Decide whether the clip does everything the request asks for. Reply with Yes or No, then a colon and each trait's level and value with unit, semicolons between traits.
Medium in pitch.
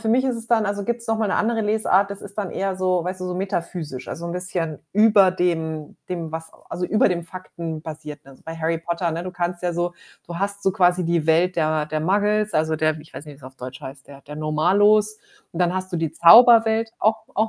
Yes: medium, 180 Hz